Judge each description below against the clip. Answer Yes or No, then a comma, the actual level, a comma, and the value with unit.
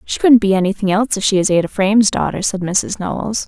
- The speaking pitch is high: Yes, high, 200 Hz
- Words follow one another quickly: Yes, fast, 240 wpm